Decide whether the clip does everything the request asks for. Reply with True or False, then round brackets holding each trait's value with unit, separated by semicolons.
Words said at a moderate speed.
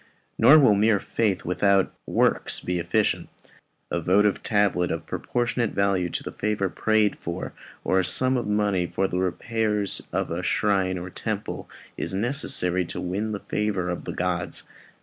True (165 wpm)